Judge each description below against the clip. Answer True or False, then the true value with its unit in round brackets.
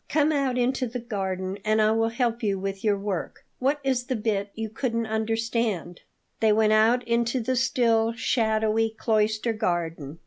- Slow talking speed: False (170 wpm)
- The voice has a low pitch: False (225 Hz)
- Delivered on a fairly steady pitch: True (2.3 semitones)